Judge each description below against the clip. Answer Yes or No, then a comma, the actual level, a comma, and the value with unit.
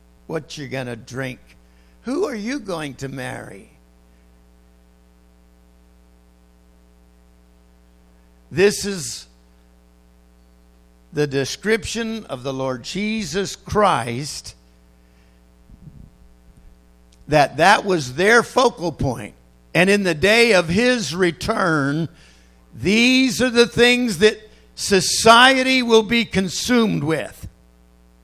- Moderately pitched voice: No, low, 120 Hz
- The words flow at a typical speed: No, slow, 90 wpm